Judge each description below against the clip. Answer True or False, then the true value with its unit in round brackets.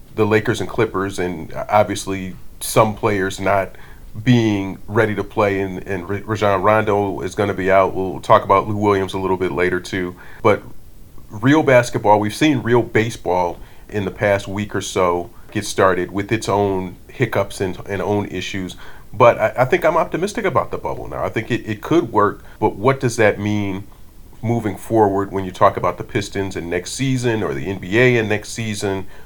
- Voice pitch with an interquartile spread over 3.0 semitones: False (2.4 semitones)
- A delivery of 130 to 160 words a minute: False (190 wpm)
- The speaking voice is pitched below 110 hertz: True (100 Hz)